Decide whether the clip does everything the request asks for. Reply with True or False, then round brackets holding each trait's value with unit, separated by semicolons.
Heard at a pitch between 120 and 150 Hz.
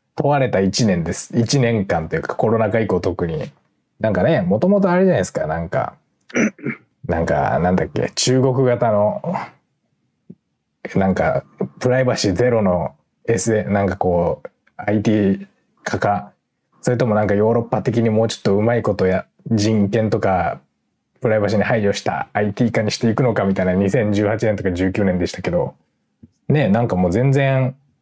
False (110 Hz)